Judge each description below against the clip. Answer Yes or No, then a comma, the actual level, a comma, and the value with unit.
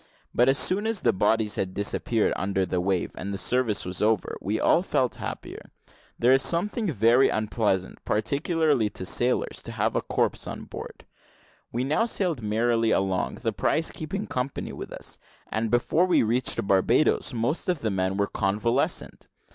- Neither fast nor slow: Yes, average, 170 wpm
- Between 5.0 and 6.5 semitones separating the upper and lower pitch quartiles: Yes, wide, 5.6 semitones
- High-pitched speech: No, low, 115 Hz